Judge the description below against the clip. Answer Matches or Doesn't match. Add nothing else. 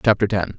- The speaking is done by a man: Matches